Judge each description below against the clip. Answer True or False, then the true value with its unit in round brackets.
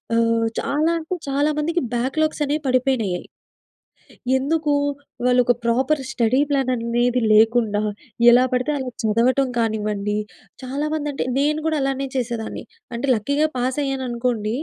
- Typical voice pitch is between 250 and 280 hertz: True (255 Hz)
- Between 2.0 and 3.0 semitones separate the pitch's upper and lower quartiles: False (3.7 semitones)